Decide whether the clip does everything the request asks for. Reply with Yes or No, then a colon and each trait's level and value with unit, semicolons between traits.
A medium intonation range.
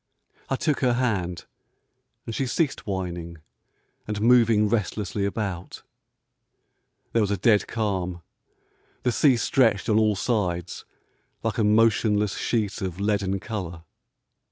Yes: average, 3.3 semitones